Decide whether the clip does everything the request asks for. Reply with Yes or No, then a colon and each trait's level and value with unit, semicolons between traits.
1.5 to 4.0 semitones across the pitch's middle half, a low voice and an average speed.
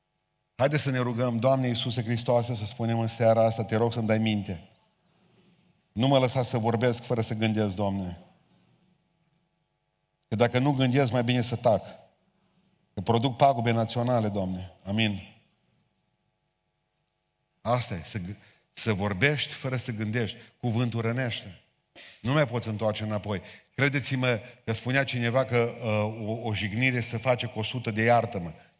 Yes: average, 3.1 semitones; low, 120 Hz; average, 150 wpm